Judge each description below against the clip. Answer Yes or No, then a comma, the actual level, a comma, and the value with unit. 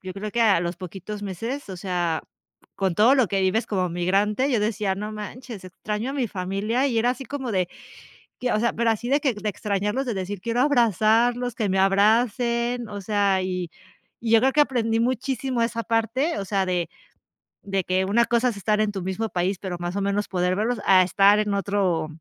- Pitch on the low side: No, high, 210 Hz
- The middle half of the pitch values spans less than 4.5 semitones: Yes, average, 3.7 semitones